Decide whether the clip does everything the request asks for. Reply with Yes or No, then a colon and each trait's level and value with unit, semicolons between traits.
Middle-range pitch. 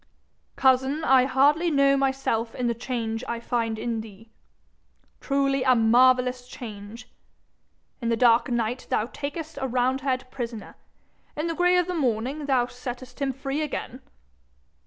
No: very high, 255 Hz